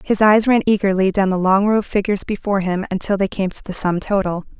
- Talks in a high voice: Yes, high, 195 Hz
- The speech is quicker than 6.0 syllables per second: Yes, 6.3 syllables/s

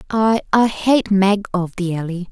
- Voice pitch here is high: Yes, high, 195 Hz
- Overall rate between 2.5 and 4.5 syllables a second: Yes, 4.1 syllables/s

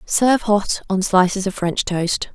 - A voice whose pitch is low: No, high, 195 Hz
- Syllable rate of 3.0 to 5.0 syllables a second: Yes, 4.2 syllables/s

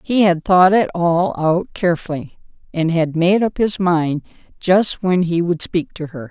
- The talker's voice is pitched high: No, medium, 175 Hz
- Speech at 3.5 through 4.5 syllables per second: Yes, 4.2 syllables/s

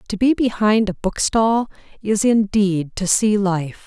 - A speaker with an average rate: Yes, average, 155 wpm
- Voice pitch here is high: Yes, high, 205 Hz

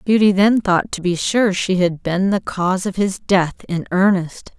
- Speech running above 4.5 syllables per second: No, 4.4 syllables/s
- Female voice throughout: Yes, female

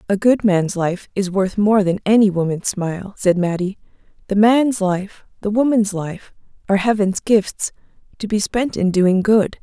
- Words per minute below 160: No, average, 175 wpm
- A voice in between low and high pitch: No, high, 200 Hz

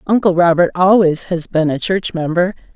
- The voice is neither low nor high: Yes, medium, 175 Hz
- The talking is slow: No, average, 175 wpm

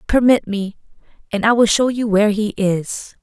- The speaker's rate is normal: Yes, average, 185 wpm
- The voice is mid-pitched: No, high, 215 Hz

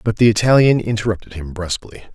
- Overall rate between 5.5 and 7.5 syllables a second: Yes, 6.6 syllables/s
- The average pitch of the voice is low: Yes, low, 105 Hz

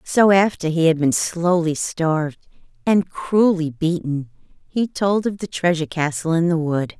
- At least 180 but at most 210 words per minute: No, average, 165 wpm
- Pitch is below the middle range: No, medium, 165 Hz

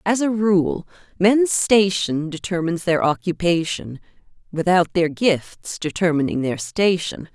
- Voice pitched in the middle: Yes, medium, 175 Hz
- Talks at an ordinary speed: No, slow, 115 wpm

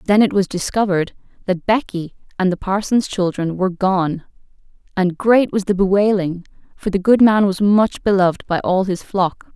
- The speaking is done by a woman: Yes, female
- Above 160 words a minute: Yes, average, 175 wpm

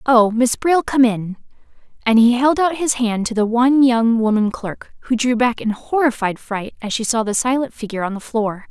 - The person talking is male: No, female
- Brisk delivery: Yes, fast, 220 wpm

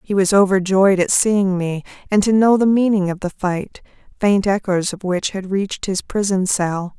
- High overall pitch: Yes, high, 195 Hz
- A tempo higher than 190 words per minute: Yes, average, 200 wpm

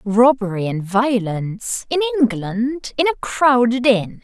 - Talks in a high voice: Yes, high, 220 Hz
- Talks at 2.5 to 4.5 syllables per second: Yes, 4.0 syllables/s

